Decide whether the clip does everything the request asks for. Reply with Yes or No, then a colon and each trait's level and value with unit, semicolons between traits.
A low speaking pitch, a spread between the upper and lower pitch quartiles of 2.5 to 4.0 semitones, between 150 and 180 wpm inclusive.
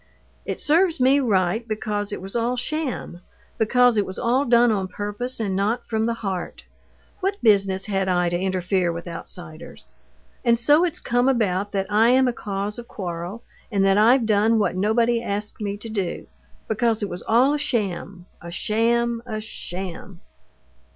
No: high, 215 Hz; average, 3.6 semitones; average, 170 wpm